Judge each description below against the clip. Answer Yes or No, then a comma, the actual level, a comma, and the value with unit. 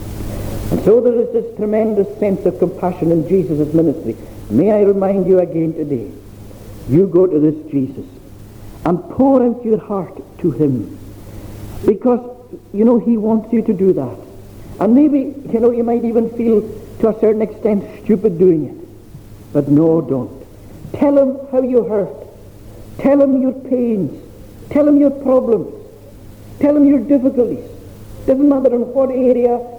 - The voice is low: No, high, 195 Hz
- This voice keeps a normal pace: Yes, average, 160 wpm